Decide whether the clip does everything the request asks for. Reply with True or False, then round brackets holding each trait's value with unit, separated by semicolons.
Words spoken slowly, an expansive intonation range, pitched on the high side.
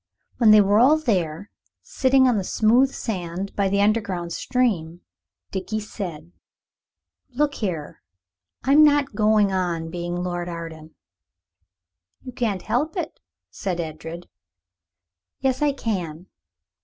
True (120 wpm; 6.1 semitones; 200 Hz)